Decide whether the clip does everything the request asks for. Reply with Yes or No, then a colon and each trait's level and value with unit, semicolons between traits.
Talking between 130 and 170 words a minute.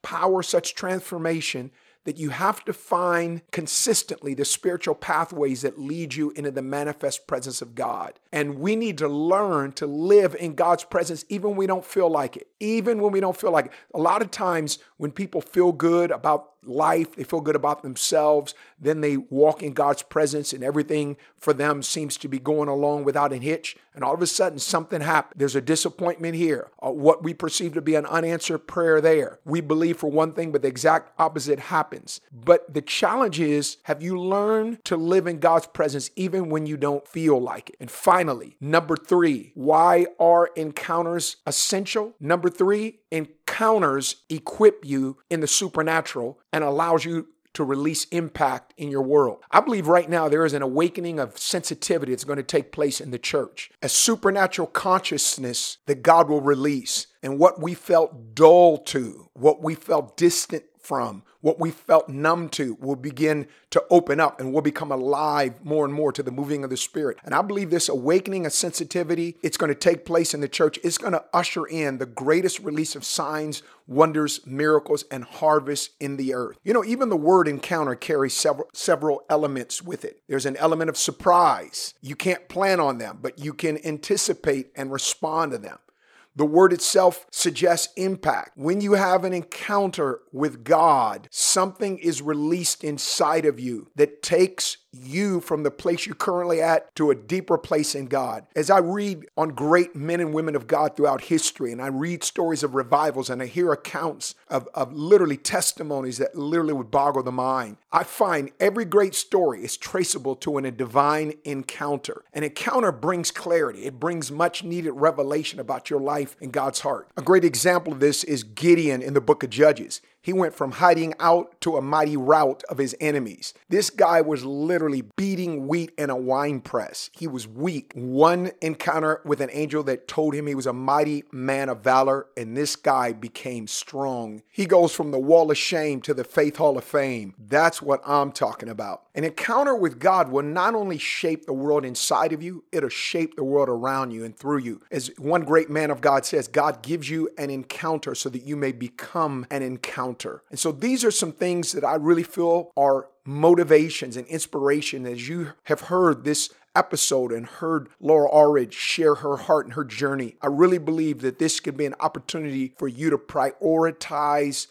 No: average, 190 wpm